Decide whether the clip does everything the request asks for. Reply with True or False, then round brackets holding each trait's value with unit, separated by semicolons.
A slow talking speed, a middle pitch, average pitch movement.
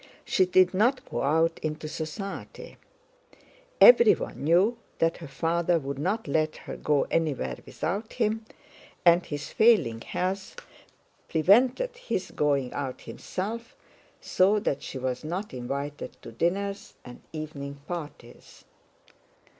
False (120 wpm; 165 Hz; 5.8 semitones)